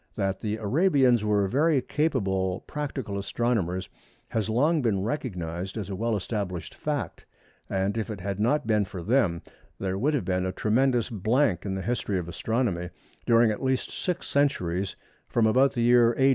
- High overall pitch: No, low, 110 Hz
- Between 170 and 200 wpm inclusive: Yes, average, 175 wpm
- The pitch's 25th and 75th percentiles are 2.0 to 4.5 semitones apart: No, average, 5.2 semitones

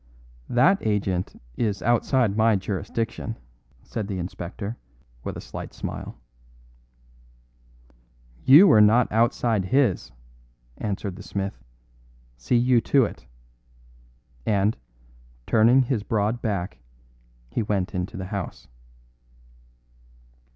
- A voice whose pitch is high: No, low, 105 Hz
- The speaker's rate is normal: No, slow, 100 wpm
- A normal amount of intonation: Yes, average, 3.3 semitones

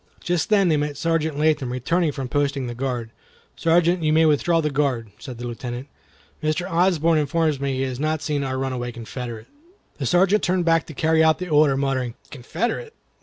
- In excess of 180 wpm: Yes, average, 190 wpm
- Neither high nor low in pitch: Yes, medium, 150 Hz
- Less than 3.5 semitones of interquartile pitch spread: No, average, 4.0 semitones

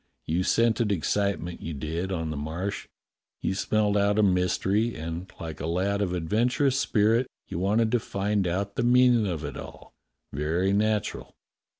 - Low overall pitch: Yes, low, 100 Hz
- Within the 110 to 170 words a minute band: Yes, average, 165 wpm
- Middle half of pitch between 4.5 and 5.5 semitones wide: No, average, 4.1 semitones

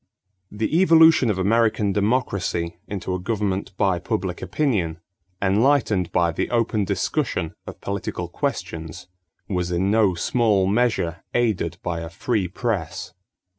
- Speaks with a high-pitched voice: No, low, 100 Hz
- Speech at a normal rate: No, slow, 130 wpm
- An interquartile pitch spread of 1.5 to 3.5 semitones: No, average, 4.2 semitones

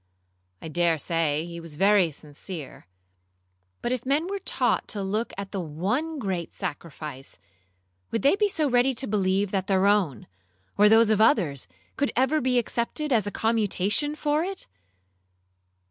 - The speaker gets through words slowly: No, average, 160 wpm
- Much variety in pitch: Yes, wide, 7.1 semitones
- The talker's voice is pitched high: Yes, high, 205 Hz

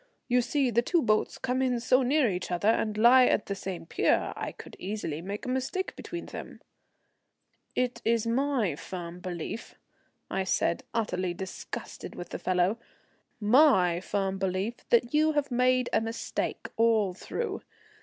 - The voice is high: Yes, high, 225 Hz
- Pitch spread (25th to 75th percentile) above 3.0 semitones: Yes, average, 5.2 semitones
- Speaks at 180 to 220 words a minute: No, average, 160 wpm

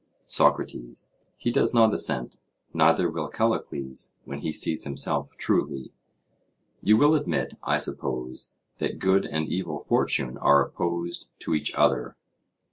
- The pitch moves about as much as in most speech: No, wide, 5.8 semitones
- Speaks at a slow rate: Yes, slow, 130 wpm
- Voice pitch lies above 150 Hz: No, very low, 80 Hz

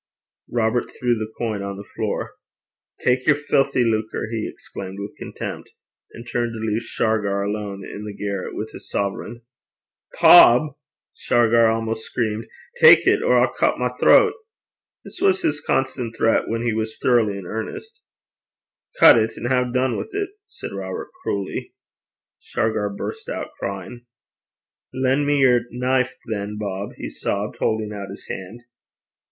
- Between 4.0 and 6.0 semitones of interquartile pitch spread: No, average, 3.3 semitones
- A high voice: No, low, 115 Hz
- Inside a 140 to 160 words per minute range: Yes, average, 155 wpm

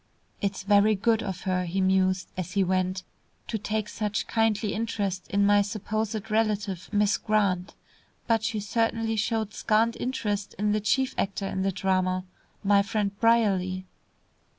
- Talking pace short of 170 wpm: Yes, average, 150 wpm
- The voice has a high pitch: Yes, high, 205 Hz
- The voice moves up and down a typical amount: No, narrow, 2.3 semitones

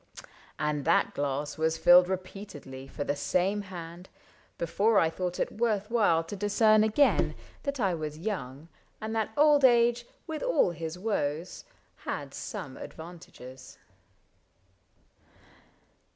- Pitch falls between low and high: Yes, medium, 180 Hz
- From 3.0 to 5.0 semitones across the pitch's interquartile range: No, wide, 5.5 semitones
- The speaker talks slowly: Yes, slow, 125 wpm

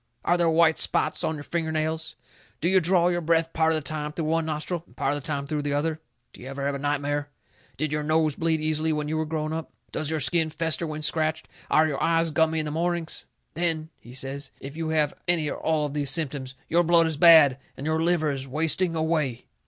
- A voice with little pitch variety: Yes, narrow, 1.7 semitones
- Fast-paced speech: Yes, fast, 240 wpm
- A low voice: No, medium, 155 Hz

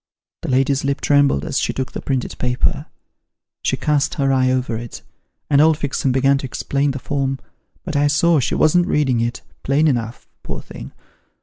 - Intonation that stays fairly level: Yes, narrow, 2.1 semitones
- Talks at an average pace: Yes, average, 190 wpm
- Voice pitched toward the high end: No, low, 135 Hz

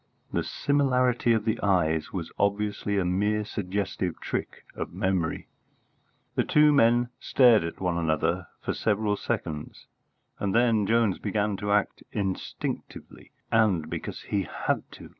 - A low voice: Yes, low, 105 Hz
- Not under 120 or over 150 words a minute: Yes, average, 140 wpm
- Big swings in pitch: No, average, 3.6 semitones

